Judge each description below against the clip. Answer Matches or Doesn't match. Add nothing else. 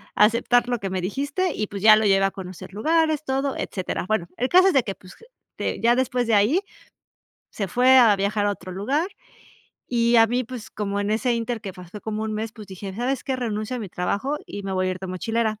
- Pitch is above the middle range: Matches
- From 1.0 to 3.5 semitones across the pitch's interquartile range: Doesn't match